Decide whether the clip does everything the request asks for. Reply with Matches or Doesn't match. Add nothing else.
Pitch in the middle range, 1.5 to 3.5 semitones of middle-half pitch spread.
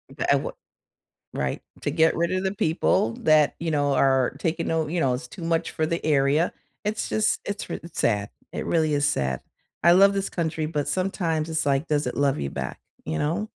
Matches